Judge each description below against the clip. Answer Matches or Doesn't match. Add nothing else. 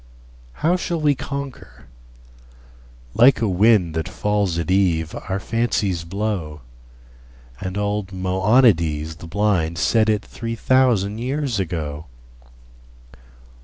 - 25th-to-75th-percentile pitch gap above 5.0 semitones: Matches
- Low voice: Matches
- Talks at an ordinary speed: Doesn't match